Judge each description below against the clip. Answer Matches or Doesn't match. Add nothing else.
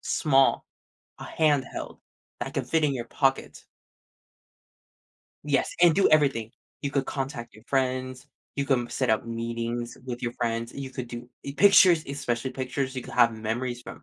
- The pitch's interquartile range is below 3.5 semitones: Matches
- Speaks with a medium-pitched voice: Doesn't match